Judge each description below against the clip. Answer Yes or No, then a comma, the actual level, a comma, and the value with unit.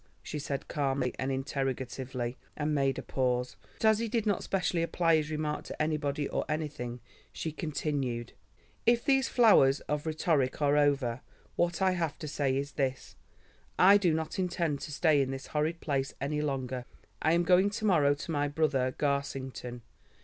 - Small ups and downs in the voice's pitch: No, average, 3.6 semitones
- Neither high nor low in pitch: Yes, medium, 145 Hz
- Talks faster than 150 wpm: Yes, average, 175 wpm